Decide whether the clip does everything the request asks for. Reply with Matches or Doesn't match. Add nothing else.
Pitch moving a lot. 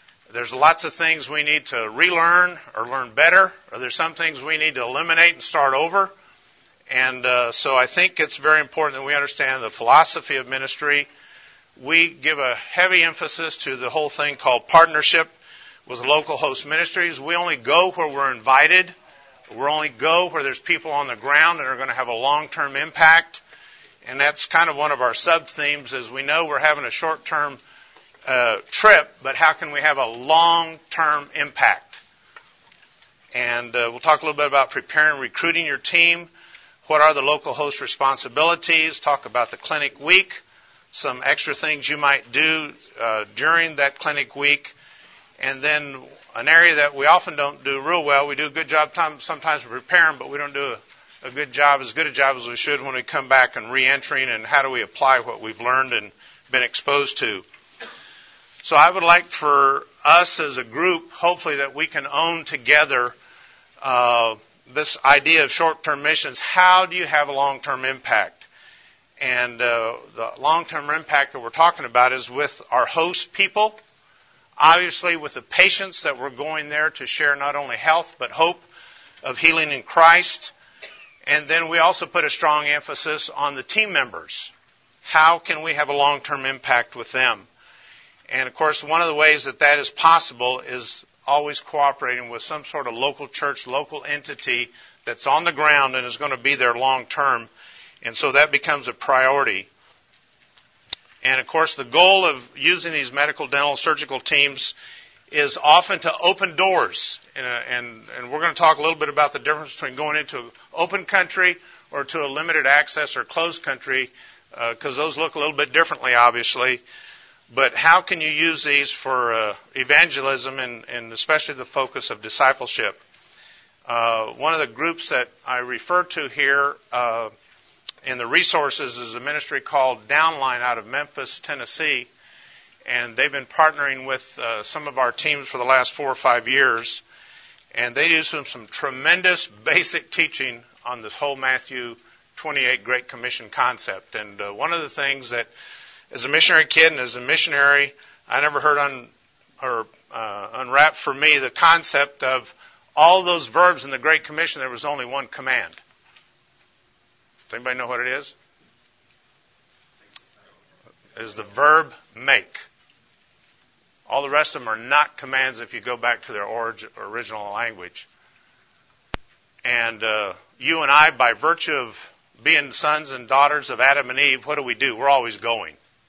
Doesn't match